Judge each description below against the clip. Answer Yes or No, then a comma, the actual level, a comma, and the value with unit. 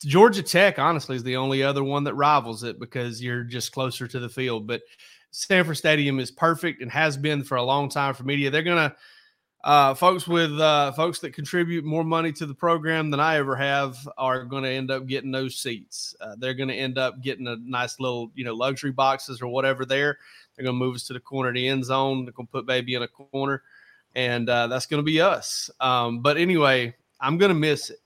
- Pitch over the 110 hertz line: Yes, low, 135 Hz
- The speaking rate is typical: No, fast, 235 wpm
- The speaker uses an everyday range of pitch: Yes, average, 3.3 semitones